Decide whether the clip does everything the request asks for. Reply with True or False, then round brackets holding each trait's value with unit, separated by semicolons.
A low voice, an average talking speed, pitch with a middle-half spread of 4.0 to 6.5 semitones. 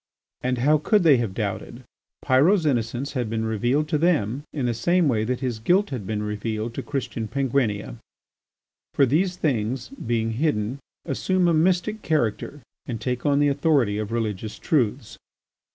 True (125 Hz; 165 wpm; 5.1 semitones)